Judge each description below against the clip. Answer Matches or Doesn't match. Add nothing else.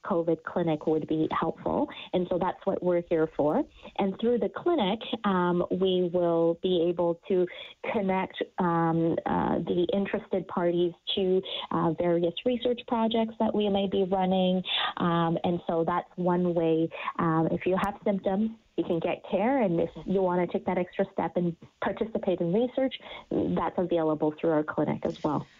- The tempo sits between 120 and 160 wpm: Doesn't match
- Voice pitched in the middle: Matches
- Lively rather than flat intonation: Doesn't match